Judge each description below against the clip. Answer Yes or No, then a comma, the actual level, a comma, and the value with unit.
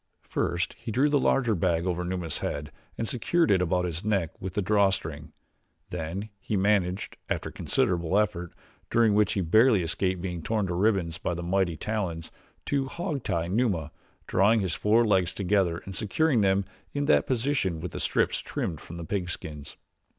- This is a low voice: Yes, very low, 95 Hz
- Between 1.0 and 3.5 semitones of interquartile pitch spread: No, average, 3.9 semitones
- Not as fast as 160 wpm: No, average, 180 wpm